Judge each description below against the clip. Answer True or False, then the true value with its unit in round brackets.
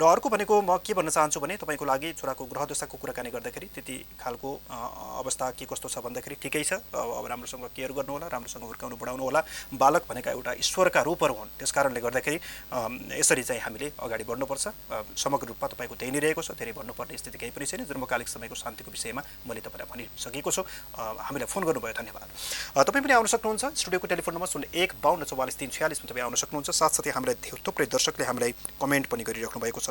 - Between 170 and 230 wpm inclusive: True (200 wpm)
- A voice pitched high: False (150 Hz)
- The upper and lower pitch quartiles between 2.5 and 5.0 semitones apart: False (5.6 semitones)